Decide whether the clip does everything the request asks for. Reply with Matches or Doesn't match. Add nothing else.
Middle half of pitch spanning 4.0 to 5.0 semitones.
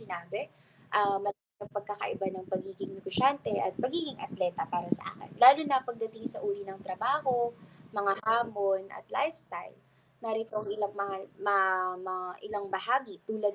Doesn't match